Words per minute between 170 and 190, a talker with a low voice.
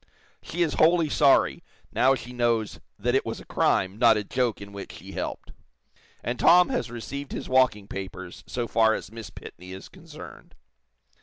Yes: average, 175 wpm; low, 120 Hz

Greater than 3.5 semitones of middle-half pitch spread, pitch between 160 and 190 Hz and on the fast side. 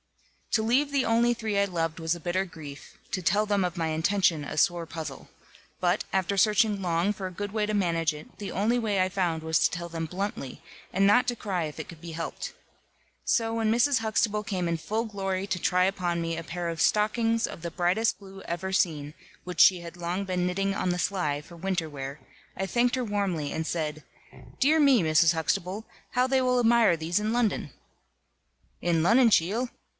Yes: average, 4.3 semitones; medium, 185 Hz; fast, 210 wpm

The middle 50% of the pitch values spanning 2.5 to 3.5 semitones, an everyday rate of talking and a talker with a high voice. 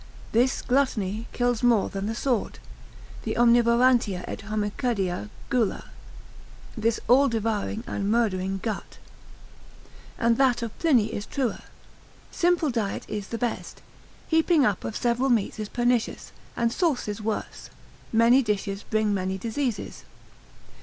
No: average, 2.9 semitones; slow, 125 wpm; high, 230 Hz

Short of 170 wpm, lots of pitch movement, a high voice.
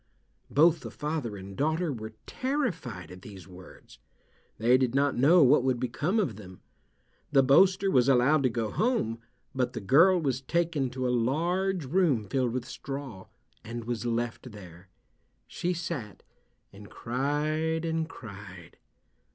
No: average, 150 wpm; wide, 6.1 semitones; low, 130 Hz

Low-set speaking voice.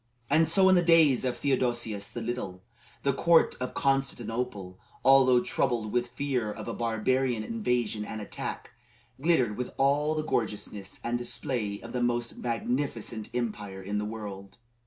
Yes: low, 120 Hz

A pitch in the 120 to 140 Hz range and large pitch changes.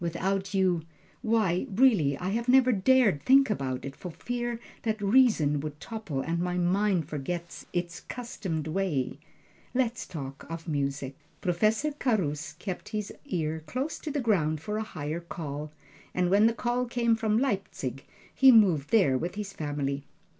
No: medium, 185 Hz; wide, 6.7 semitones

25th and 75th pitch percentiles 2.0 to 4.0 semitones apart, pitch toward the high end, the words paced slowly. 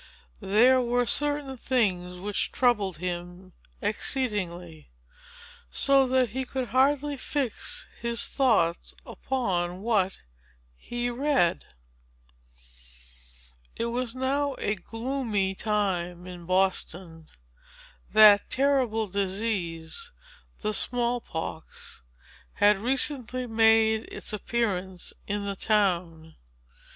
No: wide, 5.5 semitones; high, 215 Hz; slow, 95 wpm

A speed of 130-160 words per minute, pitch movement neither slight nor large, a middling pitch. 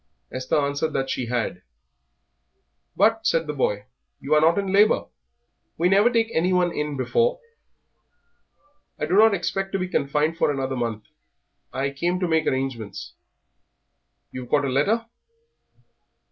No: average, 145 wpm; wide, 6.3 semitones; medium, 155 Hz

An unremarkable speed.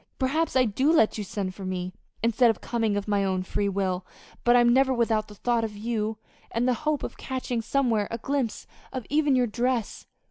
No: fast, 210 wpm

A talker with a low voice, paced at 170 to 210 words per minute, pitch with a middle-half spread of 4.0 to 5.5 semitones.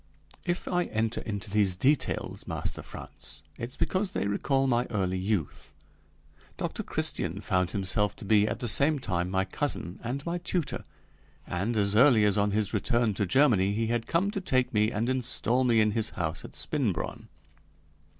Yes: low, 110 Hz; average, 175 wpm; average, 4.5 semitones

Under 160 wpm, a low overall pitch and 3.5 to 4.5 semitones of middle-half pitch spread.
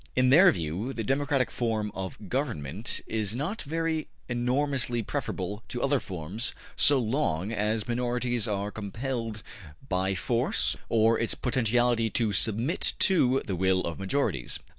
Yes: average, 140 wpm; low, 115 Hz; average, 4.2 semitones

